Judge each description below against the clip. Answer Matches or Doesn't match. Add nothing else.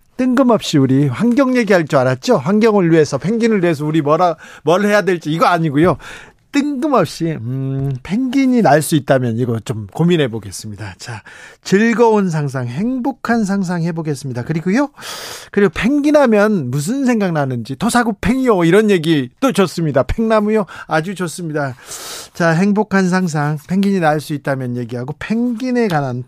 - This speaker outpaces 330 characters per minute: Matches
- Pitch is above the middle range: Doesn't match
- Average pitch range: Doesn't match